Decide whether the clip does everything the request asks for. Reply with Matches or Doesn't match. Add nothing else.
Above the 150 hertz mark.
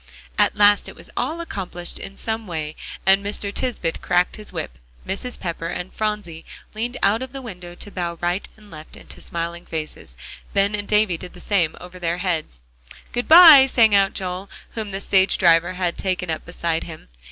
Matches